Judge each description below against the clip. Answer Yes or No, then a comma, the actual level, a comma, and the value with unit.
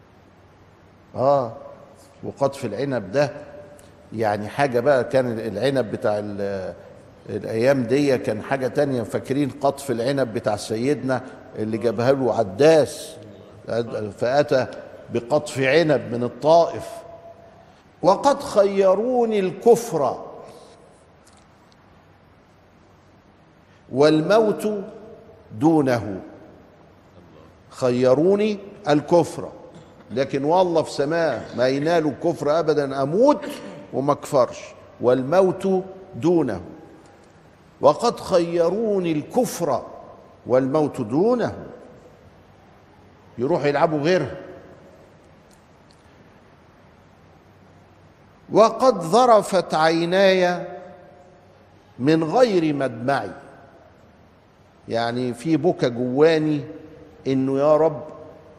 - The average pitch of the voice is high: No, medium, 145 Hz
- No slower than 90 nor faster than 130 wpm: No, average, 70 wpm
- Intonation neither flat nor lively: No, wide, 6.9 semitones